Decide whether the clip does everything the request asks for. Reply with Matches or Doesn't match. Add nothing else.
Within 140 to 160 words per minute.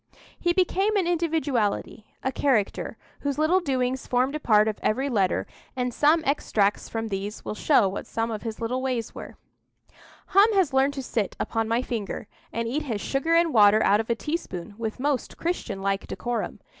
Doesn't match